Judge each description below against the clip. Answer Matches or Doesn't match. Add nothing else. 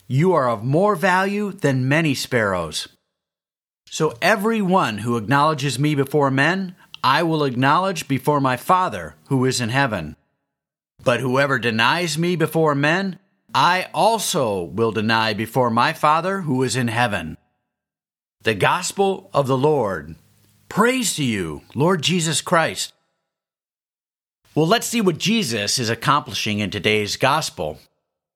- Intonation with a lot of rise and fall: Matches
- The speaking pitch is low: Doesn't match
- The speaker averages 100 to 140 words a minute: Matches